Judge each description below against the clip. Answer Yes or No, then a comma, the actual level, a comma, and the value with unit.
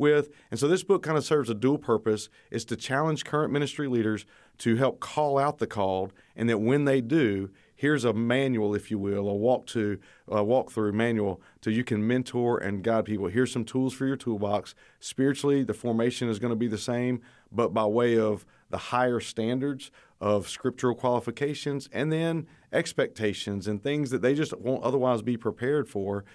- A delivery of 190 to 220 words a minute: Yes, average, 195 wpm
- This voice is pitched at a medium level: No, low, 120 Hz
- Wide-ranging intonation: No, average, 4.0 semitones